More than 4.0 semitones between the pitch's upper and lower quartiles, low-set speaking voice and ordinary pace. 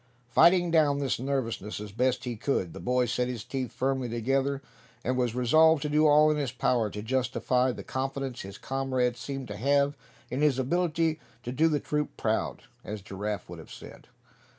No: average, 3.0 semitones; low, 130 Hz; average, 190 wpm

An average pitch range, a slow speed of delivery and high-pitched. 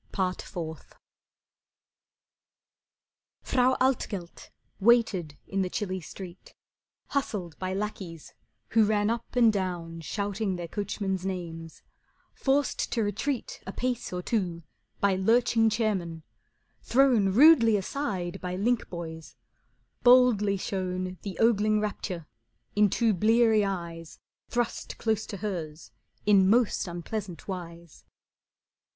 Yes: average, 4.0 semitones; slow, 110 wpm; high, 200 Hz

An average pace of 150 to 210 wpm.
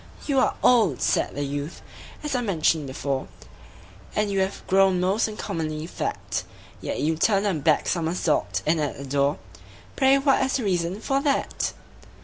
Yes: average, 165 wpm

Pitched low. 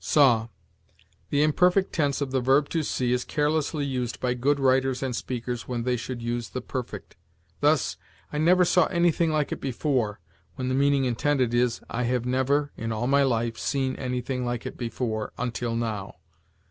Yes: low, 130 Hz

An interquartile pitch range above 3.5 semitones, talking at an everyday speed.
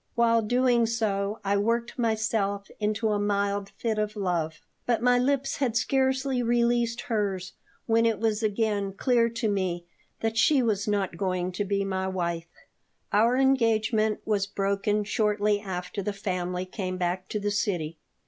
No: average, 2.8 semitones; average, 160 wpm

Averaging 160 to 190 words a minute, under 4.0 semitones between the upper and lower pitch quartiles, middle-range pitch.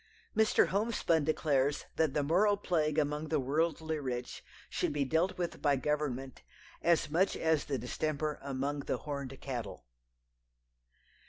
No: average, 140 wpm; narrow, 2.6 semitones; medium, 150 Hz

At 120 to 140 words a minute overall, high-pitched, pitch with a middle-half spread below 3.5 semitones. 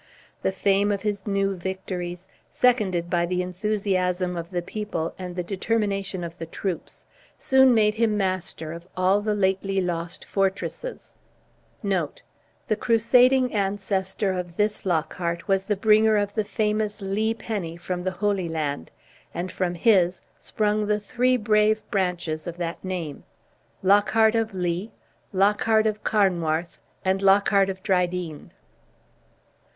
Yes: slow, 135 wpm; high, 195 Hz; average, 3.0 semitones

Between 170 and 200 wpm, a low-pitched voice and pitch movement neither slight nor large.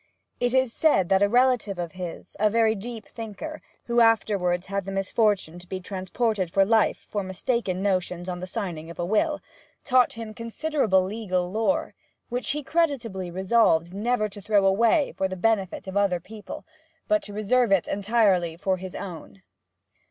No: average, 175 wpm; high, 200 Hz; average, 3.7 semitones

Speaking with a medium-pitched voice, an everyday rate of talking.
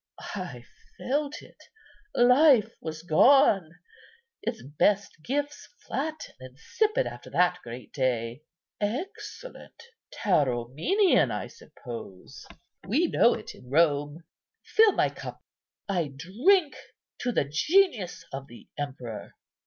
No: medium, 180 Hz; slow, 110 wpm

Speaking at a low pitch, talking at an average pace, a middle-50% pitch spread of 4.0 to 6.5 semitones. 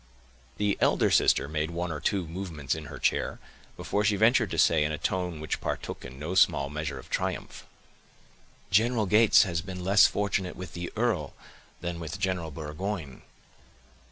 Yes: very low, 90 Hz; average, 170 wpm; average, 4.4 semitones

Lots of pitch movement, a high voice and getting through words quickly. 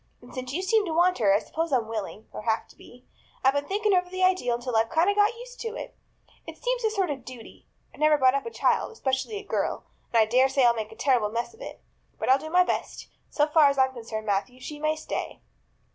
Yes: wide, 7.2 semitones; very high, 275 Hz; fast, 260 wpm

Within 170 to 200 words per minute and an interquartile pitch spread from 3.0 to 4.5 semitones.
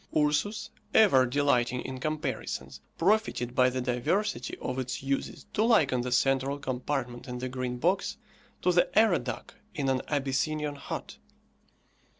No: average, 140 wpm; average, 3.3 semitones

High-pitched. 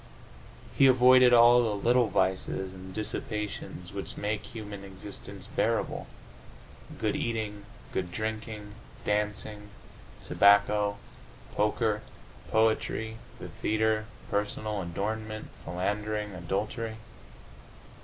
No: low, 105 Hz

